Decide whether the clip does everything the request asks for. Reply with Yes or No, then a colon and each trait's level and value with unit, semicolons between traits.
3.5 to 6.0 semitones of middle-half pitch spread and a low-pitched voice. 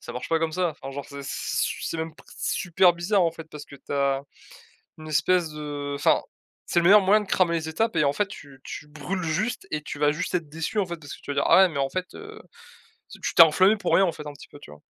No: average, 4.1 semitones; medium, 160 Hz